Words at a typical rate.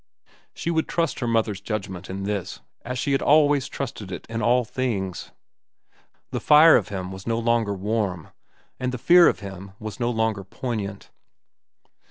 Yes: average, 170 wpm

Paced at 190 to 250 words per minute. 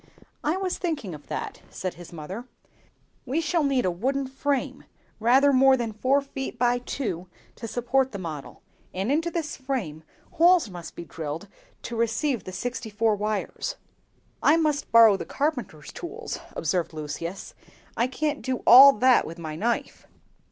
No: average, 160 wpm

